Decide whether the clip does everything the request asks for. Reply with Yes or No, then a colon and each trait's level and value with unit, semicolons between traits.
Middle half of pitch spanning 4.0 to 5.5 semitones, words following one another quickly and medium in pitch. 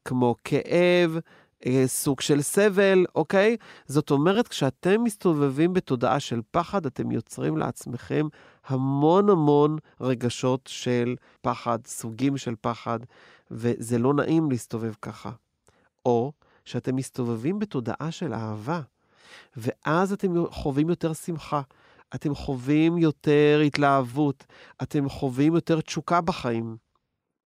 No: average, 4.8 semitones; average, 105 wpm; medium, 145 Hz